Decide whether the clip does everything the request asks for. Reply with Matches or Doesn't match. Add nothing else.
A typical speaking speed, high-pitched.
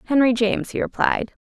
Matches